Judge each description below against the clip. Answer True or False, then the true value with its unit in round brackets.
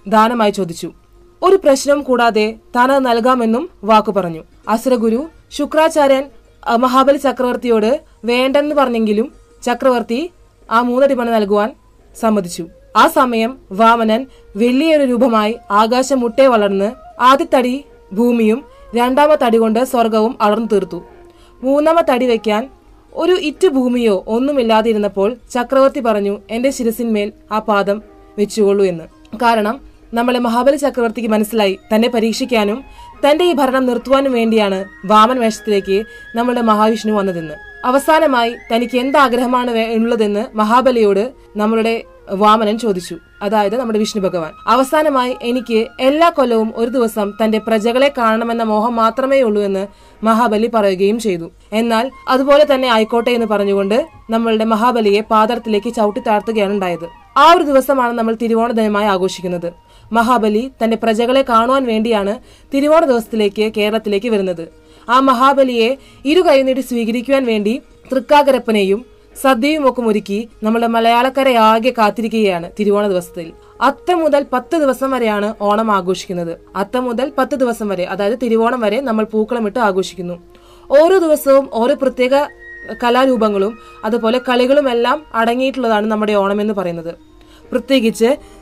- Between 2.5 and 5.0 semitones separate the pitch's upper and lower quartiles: True (3.7 semitones)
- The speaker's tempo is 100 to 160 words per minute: True (115 wpm)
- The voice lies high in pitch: True (230 Hz)